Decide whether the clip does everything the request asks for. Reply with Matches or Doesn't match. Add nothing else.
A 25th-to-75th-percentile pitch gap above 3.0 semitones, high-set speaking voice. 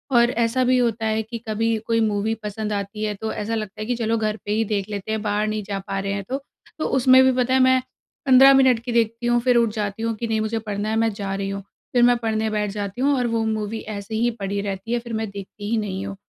Doesn't match